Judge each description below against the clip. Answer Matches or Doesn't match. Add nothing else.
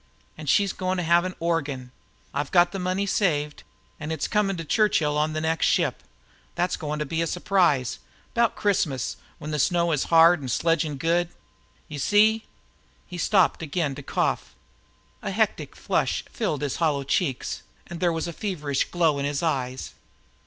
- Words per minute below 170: Doesn't match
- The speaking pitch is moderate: Matches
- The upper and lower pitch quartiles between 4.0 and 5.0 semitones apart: Doesn't match